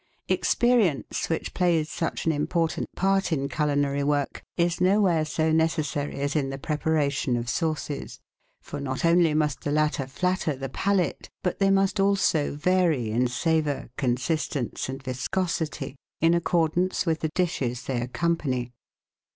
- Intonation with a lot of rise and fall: No, average, 3.7 semitones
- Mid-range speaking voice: Yes, medium, 155 Hz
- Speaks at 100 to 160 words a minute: Yes, average, 145 wpm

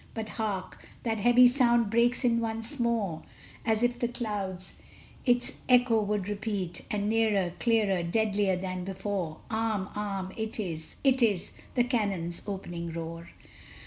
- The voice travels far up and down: No, average, 3.6 semitones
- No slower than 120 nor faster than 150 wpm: Yes, average, 145 wpm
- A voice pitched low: No, high, 210 Hz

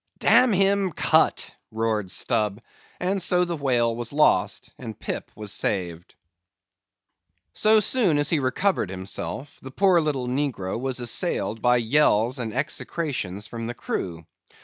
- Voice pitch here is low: Yes, low, 125 Hz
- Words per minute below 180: Yes, average, 140 wpm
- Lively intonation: Yes, wide, 7.1 semitones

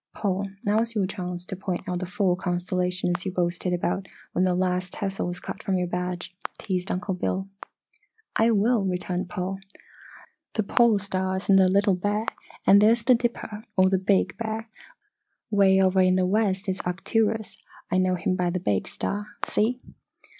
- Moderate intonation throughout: No, narrow, 2.2 semitones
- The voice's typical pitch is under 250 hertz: Yes, high, 190 Hz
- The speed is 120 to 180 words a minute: Yes, average, 170 wpm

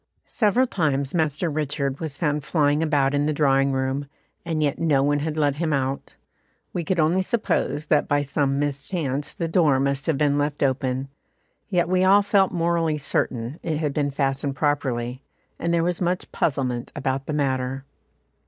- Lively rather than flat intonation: No, average, 3.1 semitones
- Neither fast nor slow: Yes, average, 175 wpm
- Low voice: No, medium, 145 Hz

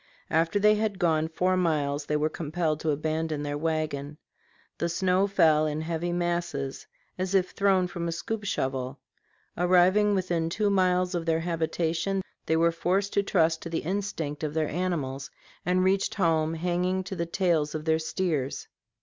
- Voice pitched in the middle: Yes, medium, 170 Hz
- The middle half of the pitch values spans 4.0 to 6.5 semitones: No, average, 2.8 semitones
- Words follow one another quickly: No, average, 170 wpm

